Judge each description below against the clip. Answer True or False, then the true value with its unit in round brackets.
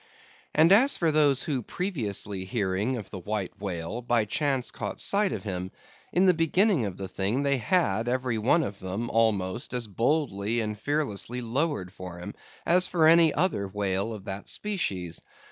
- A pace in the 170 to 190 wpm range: True (175 wpm)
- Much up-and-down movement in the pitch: True (7.7 semitones)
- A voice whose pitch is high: False (115 Hz)